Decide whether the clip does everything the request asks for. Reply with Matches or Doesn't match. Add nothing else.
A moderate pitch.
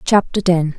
Matches